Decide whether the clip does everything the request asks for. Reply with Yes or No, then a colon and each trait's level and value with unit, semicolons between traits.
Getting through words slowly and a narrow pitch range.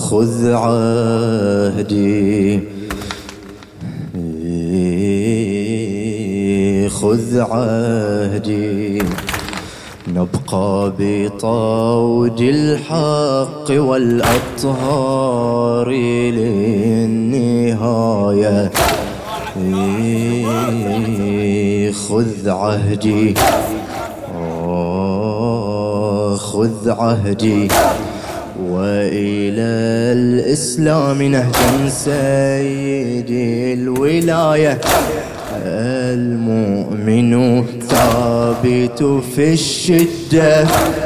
No: slow, 30 wpm; average, 3.3 semitones